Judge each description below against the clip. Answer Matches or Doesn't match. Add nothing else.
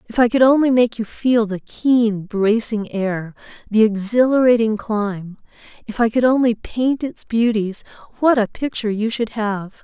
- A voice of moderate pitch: Doesn't match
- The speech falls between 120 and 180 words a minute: Matches